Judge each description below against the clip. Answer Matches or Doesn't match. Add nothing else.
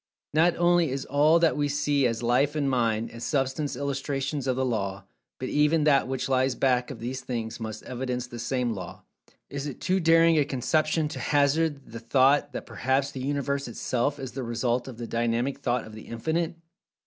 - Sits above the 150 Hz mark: Doesn't match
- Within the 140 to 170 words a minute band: Doesn't match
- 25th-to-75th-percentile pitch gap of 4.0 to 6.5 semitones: Doesn't match